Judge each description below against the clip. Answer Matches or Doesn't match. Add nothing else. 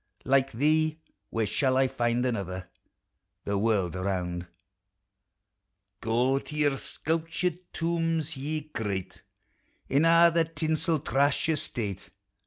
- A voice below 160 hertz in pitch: Matches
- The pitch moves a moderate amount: Doesn't match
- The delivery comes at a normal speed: Doesn't match